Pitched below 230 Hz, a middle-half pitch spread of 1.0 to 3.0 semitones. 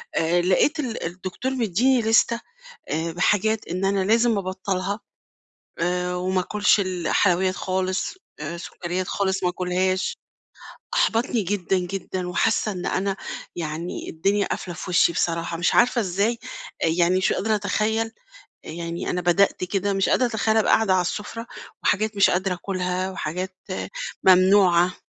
Yes: medium, 185 Hz; narrow, 2.6 semitones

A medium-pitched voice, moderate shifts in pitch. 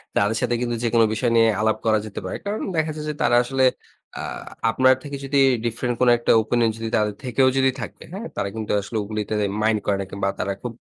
No: low, 115 Hz; average, 3.2 semitones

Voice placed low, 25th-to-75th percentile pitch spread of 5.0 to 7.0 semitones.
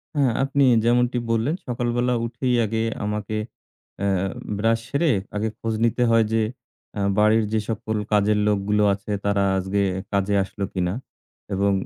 No: low, 110 Hz; average, 2.9 semitones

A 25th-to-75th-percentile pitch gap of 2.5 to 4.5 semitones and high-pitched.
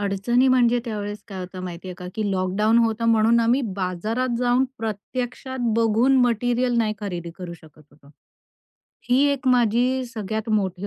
Yes: average, 3.9 semitones; high, 220 Hz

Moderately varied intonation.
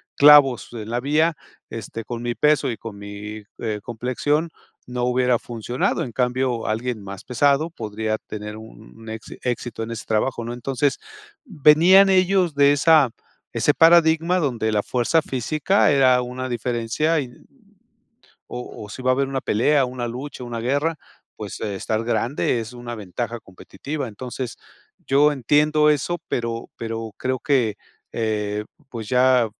Yes: average, 4.1 semitones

